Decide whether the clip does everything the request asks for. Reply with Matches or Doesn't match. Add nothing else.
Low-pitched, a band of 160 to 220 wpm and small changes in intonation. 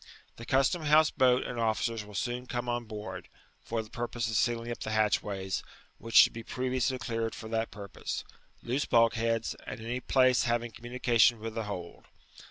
Matches